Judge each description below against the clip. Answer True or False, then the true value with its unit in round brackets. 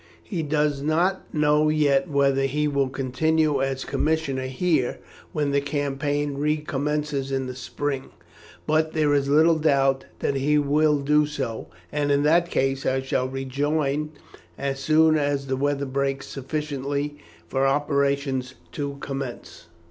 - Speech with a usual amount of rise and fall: False (1.7 semitones)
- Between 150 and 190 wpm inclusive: False (140 wpm)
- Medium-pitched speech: True (145 Hz)